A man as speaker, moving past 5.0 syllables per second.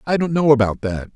Yes: male; 5.8 syllables/s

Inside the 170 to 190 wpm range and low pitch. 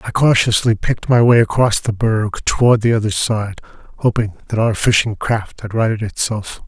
Yes: average, 180 wpm; low, 110 Hz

